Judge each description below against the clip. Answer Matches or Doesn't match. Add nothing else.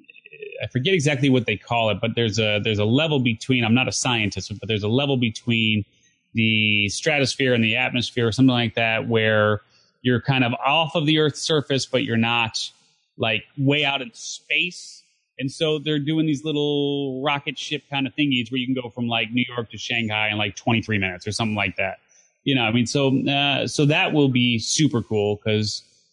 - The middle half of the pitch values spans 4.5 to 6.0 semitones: Doesn't match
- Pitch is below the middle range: Matches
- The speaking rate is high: Matches